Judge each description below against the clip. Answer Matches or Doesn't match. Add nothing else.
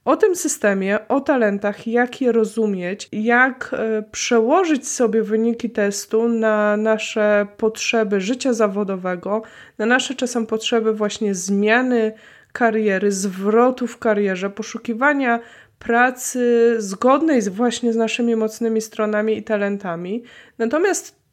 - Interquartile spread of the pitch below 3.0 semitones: Matches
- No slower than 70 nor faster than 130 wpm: Matches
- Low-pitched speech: Doesn't match